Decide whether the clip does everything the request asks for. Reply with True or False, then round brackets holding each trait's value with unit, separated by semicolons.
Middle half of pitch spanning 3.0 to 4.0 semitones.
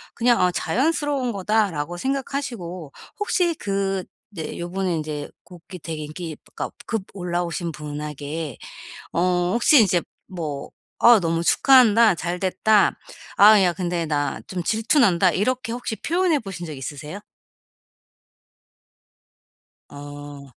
False (5.6 semitones)